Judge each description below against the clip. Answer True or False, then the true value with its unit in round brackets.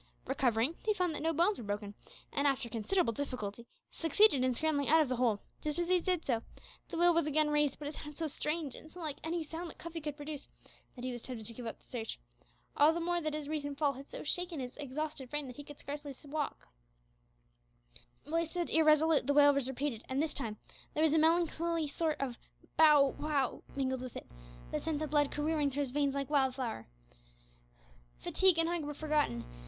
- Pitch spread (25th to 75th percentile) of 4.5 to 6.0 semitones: False (3.3 semitones)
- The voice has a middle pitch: False (295 Hz)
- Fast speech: True (215 wpm)